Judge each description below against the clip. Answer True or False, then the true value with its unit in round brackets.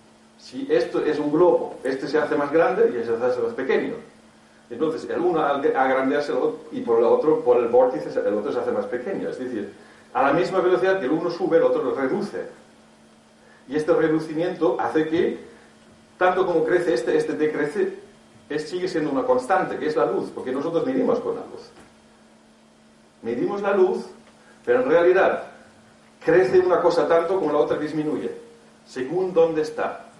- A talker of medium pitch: True (180 Hz)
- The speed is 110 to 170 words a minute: False (180 wpm)